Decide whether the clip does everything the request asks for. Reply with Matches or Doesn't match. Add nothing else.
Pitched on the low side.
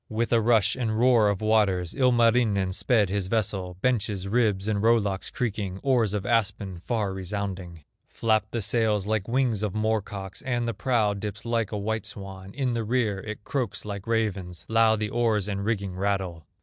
Matches